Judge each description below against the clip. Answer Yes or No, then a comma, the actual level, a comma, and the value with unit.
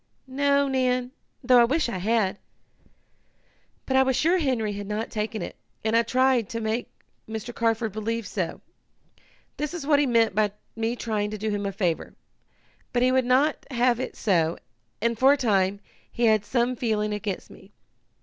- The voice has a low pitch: No, high, 230 Hz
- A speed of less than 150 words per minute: No, average, 180 wpm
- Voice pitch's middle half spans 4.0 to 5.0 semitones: No, average, 3.4 semitones